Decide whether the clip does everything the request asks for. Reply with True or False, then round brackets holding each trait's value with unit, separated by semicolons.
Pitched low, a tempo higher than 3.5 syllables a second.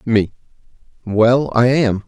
False (115 Hz; 3.2 syllables/s)